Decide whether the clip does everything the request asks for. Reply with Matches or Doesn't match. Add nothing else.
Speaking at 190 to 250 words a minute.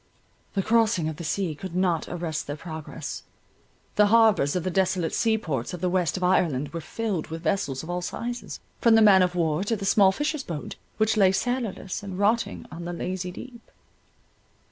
Matches